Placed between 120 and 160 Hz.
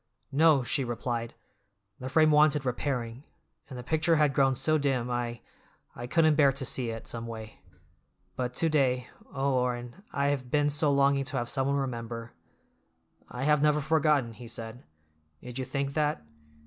Yes: low, 135 Hz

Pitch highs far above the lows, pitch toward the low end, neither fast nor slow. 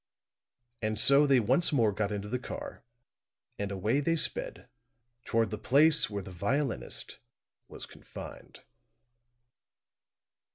No: wide, 5.7 semitones; low, 115 Hz; slow, 120 wpm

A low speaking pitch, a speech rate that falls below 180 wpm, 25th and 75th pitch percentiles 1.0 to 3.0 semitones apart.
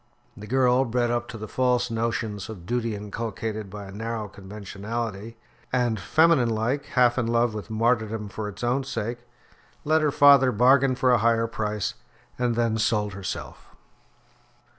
Yes: low, 115 Hz; average, 160 wpm; average, 2.7 semitones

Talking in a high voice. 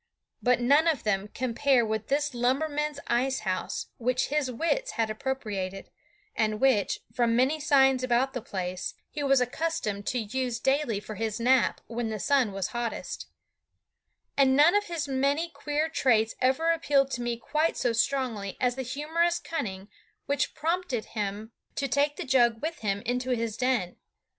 Yes: very high, 255 Hz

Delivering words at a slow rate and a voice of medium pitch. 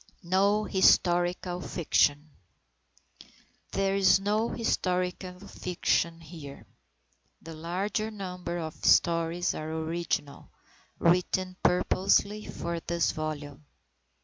Yes: slow, 95 wpm; medium, 175 Hz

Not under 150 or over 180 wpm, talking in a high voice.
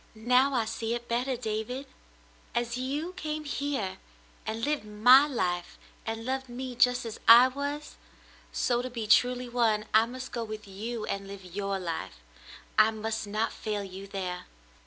Yes: average, 170 wpm; high, 230 Hz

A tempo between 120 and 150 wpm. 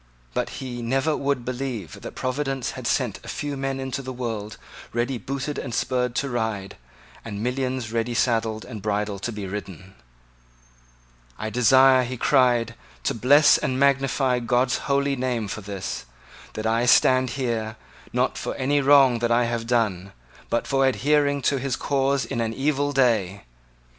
No: average, 165 wpm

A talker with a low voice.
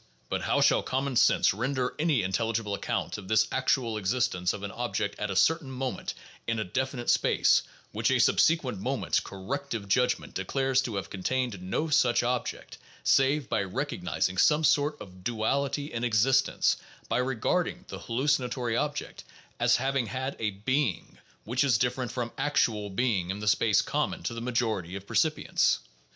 Yes: low, 120 Hz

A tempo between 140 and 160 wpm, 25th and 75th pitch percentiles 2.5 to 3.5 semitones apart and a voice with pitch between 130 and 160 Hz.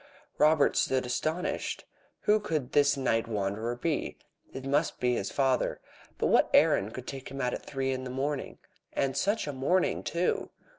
No: average, 170 wpm; average, 3.2 semitones; low, 135 Hz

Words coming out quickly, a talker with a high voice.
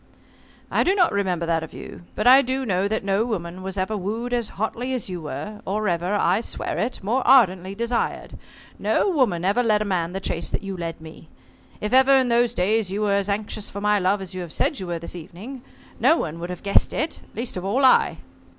Yes: fast, 230 wpm; high, 200 Hz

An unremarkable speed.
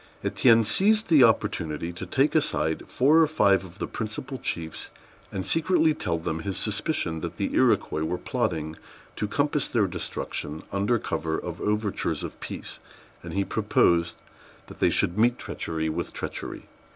Yes: average, 160 wpm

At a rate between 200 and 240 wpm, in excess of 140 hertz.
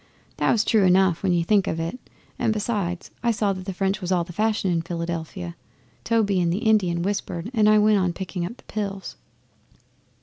Yes: fast, 205 wpm; high, 190 Hz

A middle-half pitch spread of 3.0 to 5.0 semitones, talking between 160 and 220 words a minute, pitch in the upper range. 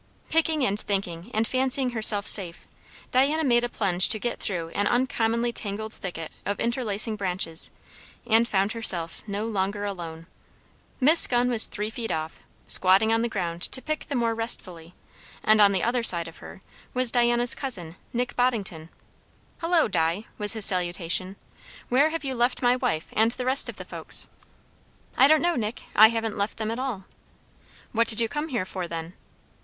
Yes: average, 4.5 semitones; average, 180 wpm; high, 220 Hz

